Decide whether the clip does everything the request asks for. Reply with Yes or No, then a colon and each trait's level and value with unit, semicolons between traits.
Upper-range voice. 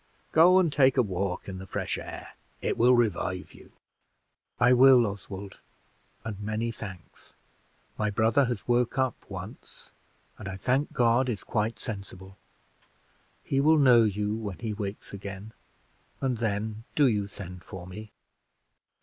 No: low, 110 Hz